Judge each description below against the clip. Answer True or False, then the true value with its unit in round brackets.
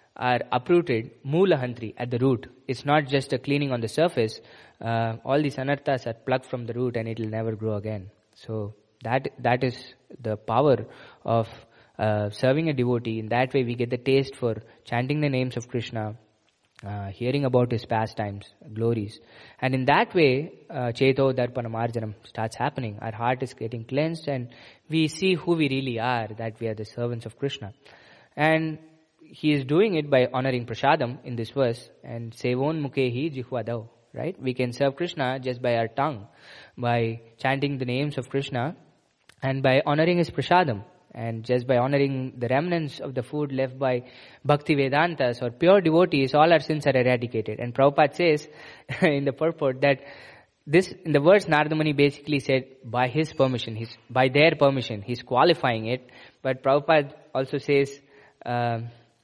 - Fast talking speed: False (175 wpm)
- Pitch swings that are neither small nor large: True (3.6 semitones)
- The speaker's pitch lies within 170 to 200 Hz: False (130 Hz)